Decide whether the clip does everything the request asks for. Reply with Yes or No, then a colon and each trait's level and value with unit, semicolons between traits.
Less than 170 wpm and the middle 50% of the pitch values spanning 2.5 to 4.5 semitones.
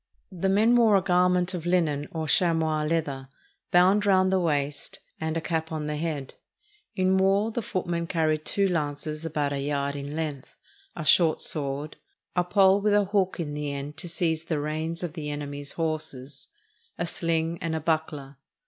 No: average, 180 wpm; average, 3.4 semitones